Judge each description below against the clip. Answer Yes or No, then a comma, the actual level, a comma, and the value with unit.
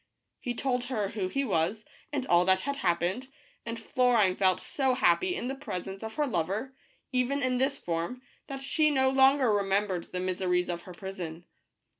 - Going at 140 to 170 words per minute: No, average, 180 wpm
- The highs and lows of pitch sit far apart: Yes, wide, 6.3 semitones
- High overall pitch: Yes, high, 220 Hz